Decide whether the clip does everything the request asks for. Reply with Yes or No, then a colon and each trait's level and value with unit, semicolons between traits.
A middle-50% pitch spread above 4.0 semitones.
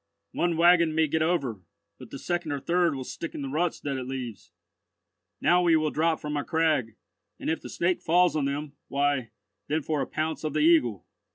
No: average, 3.1 semitones